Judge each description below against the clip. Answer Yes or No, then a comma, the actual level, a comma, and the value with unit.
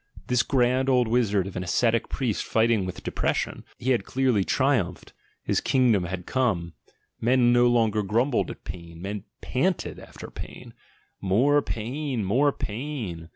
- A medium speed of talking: Yes, average, 155 wpm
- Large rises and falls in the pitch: No, average, 4.8 semitones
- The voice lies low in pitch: Yes, low, 115 Hz